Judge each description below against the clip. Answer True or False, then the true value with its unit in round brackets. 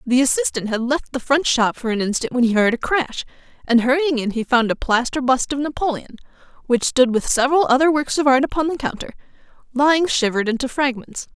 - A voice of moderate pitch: False (260 Hz)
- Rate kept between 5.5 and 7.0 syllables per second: True (5.9 syllables/s)